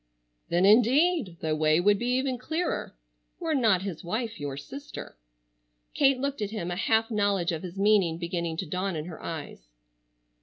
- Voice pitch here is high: Yes, high, 195 Hz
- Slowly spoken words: No, average, 165 wpm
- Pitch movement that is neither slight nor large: No, wide, 6.4 semitones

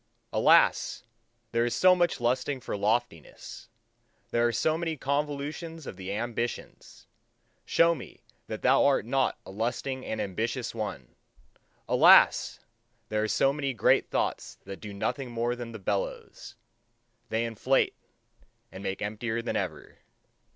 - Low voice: Yes, low, 120 Hz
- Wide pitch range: No, average, 4.1 semitones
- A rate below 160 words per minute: Yes, average, 140 wpm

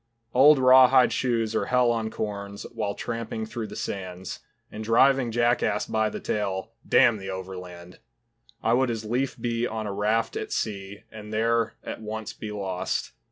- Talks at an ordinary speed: Yes, average, 170 wpm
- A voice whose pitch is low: Yes, low, 110 Hz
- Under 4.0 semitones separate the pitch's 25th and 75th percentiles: Yes, average, 2.7 semitones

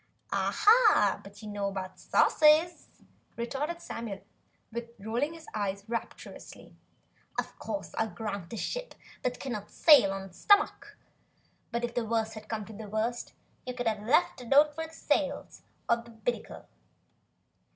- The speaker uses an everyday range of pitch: No, wide, 5.9 semitones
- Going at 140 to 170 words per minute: Yes, average, 150 wpm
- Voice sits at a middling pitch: No, high, 230 Hz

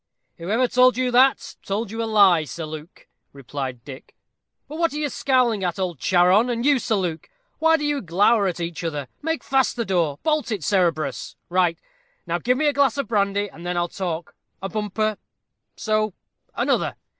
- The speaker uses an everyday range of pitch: No, wide, 6.5 semitones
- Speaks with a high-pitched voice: Yes, high, 205 Hz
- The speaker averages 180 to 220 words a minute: Yes, average, 190 wpm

